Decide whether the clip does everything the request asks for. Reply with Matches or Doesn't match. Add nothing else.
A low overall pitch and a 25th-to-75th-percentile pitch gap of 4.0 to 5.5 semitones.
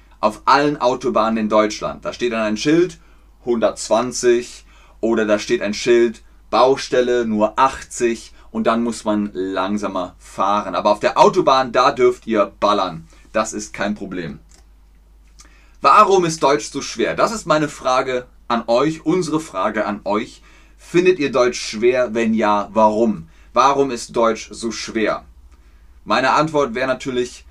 Matches